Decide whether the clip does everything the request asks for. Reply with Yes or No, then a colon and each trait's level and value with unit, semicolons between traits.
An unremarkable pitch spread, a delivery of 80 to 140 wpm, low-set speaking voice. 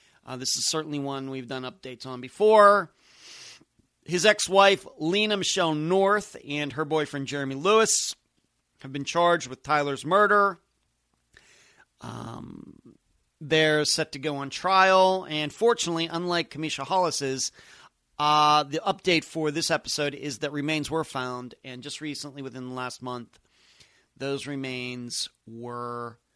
No: average, 4.5 semitones; slow, 135 wpm; medium, 150 Hz